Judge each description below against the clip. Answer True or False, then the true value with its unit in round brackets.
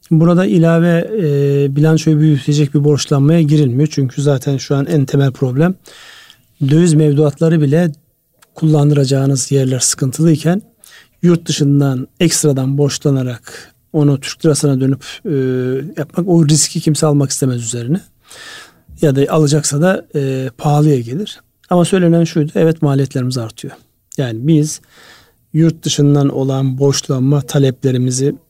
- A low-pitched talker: False (150 Hz)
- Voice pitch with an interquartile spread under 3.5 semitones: True (2.9 semitones)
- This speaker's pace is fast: False (120 wpm)